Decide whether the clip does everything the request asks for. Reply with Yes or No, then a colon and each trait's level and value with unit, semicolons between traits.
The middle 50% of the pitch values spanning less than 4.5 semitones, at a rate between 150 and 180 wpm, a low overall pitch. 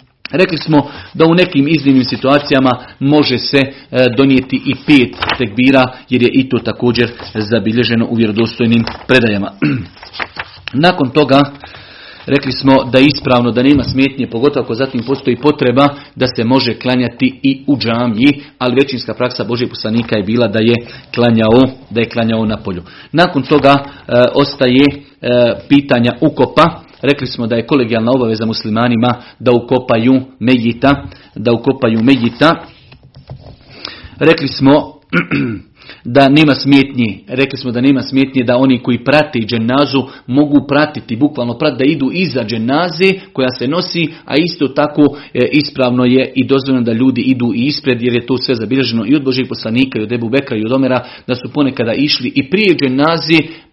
Yes: average, 2.8 semitones; average, 155 wpm; low, 130 Hz